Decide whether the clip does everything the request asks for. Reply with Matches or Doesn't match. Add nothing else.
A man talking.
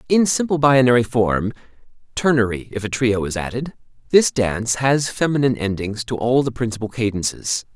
Matches